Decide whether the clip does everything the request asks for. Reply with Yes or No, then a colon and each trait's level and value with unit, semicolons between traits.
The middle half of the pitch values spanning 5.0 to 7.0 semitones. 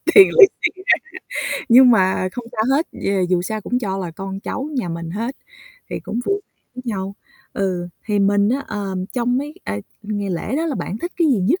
Yes: wide, 5.5 semitones